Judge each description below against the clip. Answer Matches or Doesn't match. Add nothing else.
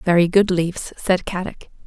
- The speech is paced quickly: Doesn't match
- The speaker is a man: Doesn't match